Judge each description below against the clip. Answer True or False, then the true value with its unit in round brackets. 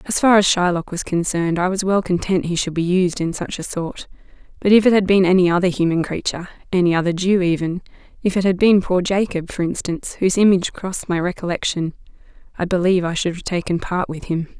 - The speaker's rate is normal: False (210 wpm)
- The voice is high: False (180 Hz)